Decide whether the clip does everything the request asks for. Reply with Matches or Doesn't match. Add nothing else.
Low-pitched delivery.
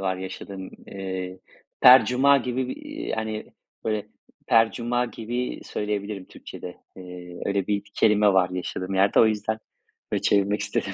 Matches